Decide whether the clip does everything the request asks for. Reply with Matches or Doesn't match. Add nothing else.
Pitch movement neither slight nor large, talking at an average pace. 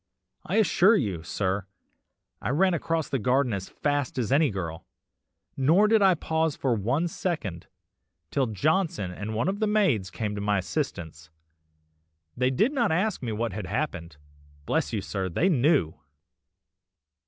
Doesn't match